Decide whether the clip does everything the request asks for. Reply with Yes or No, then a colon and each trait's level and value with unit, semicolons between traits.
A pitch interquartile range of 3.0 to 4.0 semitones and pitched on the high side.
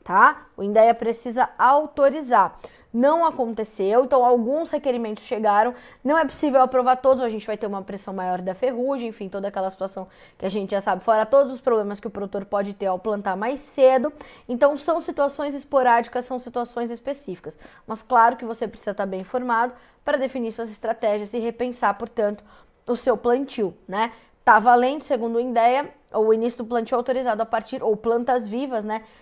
Yes: average, 3.3 semitones; high, 235 Hz